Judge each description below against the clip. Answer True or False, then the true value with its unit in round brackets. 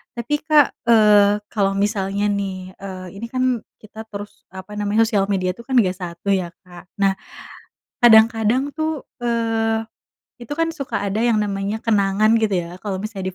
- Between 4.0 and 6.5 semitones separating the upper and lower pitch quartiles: False (2.9 semitones)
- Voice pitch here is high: True (210 Hz)